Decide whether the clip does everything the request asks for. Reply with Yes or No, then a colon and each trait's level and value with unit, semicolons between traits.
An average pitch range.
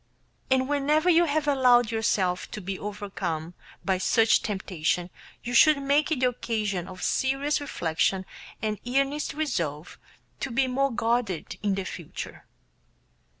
No: wide, 6.5 semitones